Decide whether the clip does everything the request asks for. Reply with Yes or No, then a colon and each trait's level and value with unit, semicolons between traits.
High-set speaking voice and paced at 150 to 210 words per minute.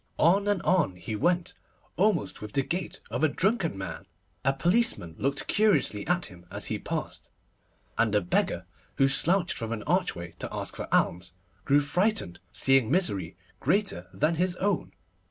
No: medium, 145 Hz; average, 165 wpm